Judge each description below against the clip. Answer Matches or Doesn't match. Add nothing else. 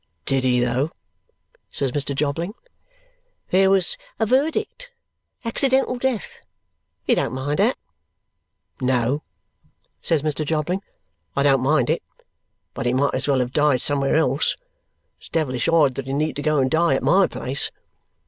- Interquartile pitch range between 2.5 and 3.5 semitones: Doesn't match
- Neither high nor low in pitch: Matches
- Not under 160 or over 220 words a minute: Doesn't match